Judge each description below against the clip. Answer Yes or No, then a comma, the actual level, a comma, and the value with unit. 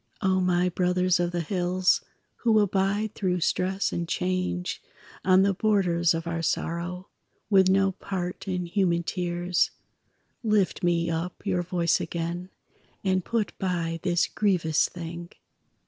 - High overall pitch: No, medium, 180 Hz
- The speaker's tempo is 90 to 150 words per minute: Yes, slow, 135 wpm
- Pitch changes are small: Yes, narrow, 1.7 semitones